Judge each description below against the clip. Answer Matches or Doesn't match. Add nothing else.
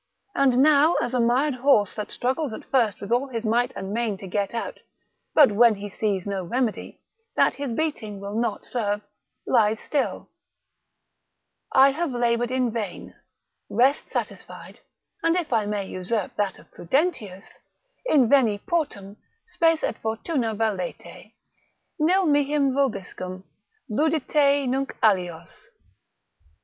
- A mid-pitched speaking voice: Doesn't match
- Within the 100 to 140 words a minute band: Matches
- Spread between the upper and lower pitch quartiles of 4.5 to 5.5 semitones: Matches